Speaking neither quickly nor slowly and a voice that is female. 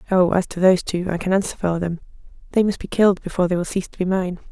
No: fast, 280 wpm; female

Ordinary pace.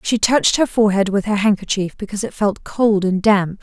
No: fast, 215 wpm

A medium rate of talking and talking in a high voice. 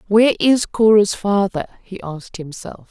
Yes: average, 145 wpm; high, 200 Hz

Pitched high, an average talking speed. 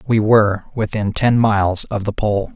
No: low, 105 Hz; average, 190 wpm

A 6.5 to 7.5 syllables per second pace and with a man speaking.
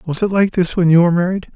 Yes: 7.0 syllables/s; male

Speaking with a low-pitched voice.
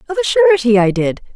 No: very high, 275 Hz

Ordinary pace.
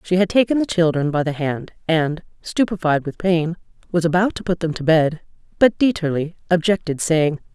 Yes: average, 185 wpm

